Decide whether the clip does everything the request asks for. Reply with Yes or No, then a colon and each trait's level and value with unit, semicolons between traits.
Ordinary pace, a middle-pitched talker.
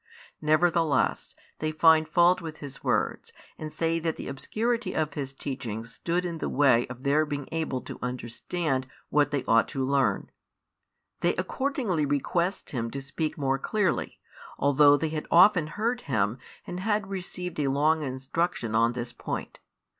Yes: average, 160 wpm; medium, 150 Hz